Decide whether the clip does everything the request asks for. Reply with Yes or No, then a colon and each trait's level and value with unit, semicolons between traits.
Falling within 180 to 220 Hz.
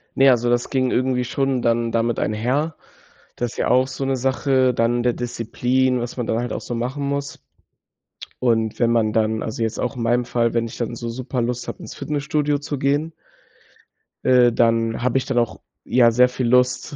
No: low, 125 Hz